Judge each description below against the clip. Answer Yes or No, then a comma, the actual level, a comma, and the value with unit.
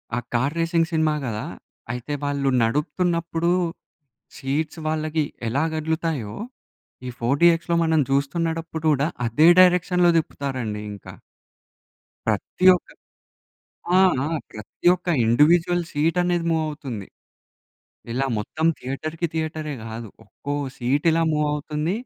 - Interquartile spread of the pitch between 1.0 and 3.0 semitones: No, average, 3.5 semitones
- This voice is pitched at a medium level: Yes, medium, 155 Hz